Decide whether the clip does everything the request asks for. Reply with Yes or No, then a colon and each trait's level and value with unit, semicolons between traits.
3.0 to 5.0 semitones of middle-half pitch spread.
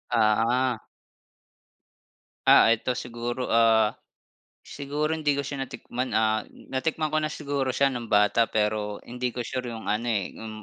Yes: average, 3.3 semitones